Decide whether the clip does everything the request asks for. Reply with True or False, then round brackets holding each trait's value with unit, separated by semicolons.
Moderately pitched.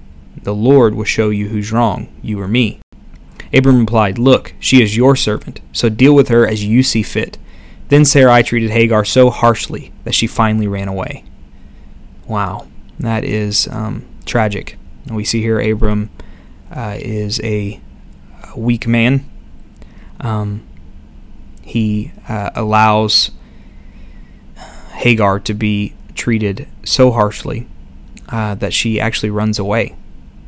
False (110 Hz)